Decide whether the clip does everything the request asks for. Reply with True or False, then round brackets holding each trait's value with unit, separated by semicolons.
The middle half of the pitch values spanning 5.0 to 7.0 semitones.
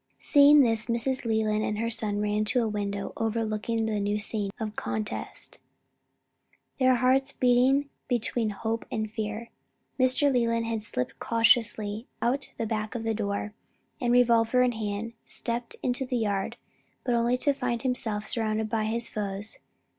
False (2.5 semitones)